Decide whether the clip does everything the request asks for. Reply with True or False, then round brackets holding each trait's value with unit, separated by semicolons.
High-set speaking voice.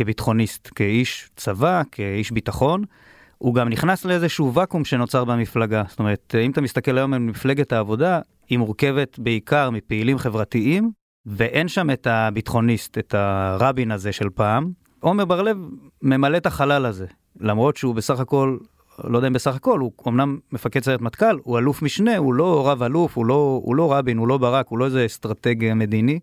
False (125 Hz)